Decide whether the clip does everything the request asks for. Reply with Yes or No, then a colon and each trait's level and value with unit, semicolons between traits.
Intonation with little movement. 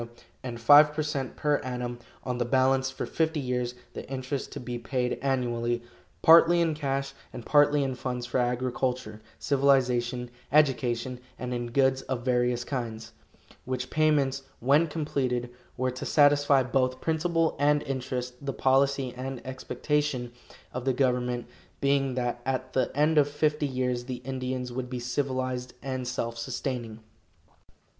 Yes: narrow, 2.1 semitones